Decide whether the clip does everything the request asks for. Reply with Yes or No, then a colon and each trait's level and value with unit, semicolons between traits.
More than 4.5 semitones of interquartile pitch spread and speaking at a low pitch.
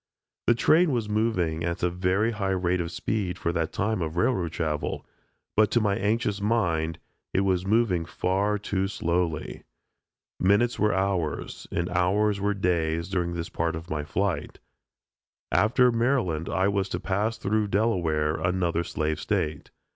No: average, 3.8 semitones; very low, 95 Hz